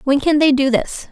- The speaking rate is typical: No, fast, 270 wpm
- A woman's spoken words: Yes, female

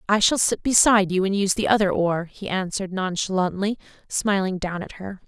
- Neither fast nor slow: Yes, average, 195 wpm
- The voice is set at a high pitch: Yes, high, 195 Hz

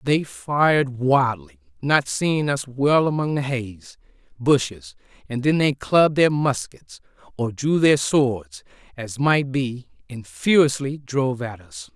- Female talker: Yes, female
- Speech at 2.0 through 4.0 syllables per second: Yes, 3.9 syllables/s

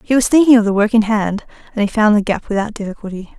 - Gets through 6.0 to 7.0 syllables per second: Yes, 6.7 syllables/s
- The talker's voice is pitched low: No, high, 215 Hz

